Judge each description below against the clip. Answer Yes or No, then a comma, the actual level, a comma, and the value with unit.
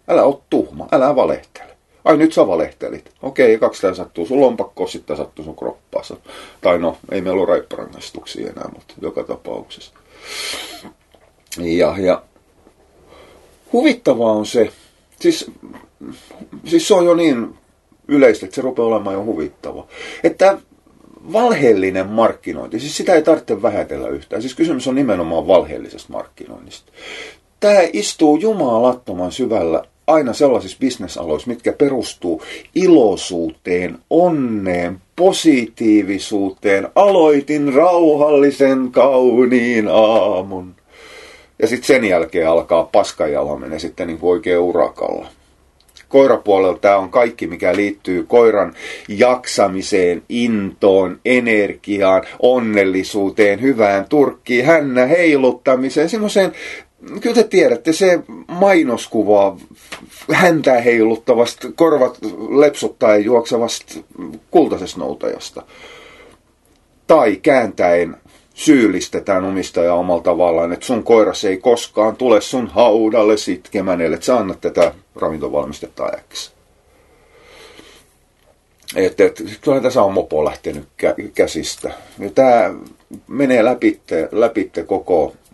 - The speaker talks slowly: No, average, 105 wpm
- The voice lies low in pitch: Yes, low, 125 Hz